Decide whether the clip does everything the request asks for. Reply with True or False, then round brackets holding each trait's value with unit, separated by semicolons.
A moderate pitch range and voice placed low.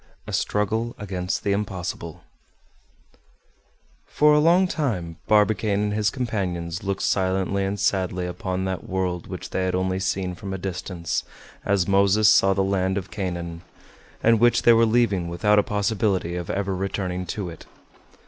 False (2.3 semitones; 95 Hz)